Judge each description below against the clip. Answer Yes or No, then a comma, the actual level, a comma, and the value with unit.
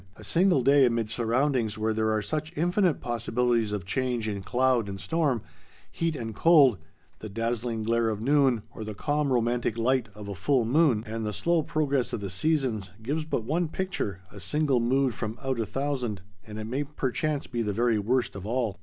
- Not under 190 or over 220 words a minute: Yes, average, 200 wpm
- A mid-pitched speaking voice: No, low, 120 Hz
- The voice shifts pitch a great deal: No, average, 4.6 semitones